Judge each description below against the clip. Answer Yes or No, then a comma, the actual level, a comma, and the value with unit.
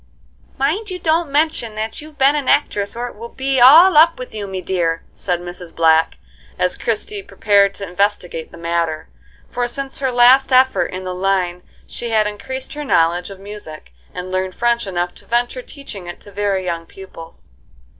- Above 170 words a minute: Yes, average, 185 wpm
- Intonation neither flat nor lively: No, wide, 6.6 semitones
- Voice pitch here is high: Yes, high, 210 Hz